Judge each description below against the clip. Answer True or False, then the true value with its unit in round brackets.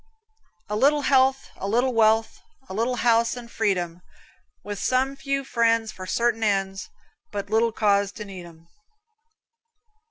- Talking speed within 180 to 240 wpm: False (145 wpm)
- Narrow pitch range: False (3.6 semitones)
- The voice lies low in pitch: False (225 Hz)